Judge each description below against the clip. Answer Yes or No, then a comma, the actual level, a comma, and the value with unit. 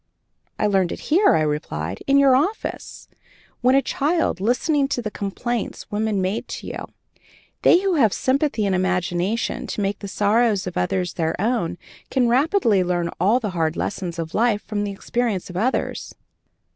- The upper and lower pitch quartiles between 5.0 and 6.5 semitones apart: Yes, wide, 5.4 semitones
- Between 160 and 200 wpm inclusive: Yes, average, 170 wpm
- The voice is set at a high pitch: Yes, high, 210 Hz